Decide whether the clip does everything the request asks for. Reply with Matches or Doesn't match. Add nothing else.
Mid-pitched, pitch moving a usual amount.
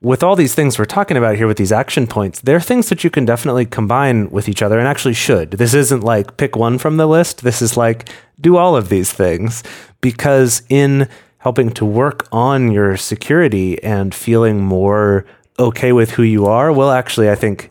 Doesn't match